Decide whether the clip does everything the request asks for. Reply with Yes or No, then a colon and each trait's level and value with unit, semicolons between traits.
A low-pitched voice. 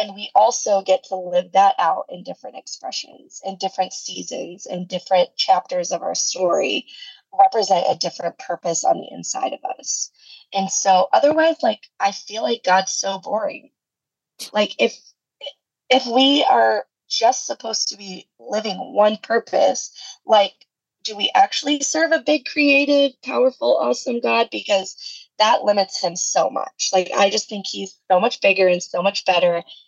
No: high, 210 Hz